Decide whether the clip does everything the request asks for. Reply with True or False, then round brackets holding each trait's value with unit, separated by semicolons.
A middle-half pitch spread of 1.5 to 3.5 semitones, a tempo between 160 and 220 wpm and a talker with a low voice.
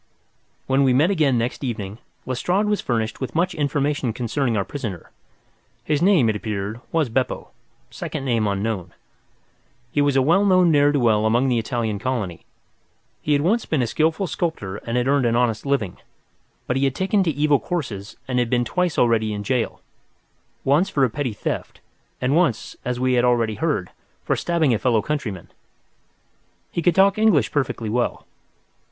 False (5.0 semitones; 175 wpm; 130 Hz)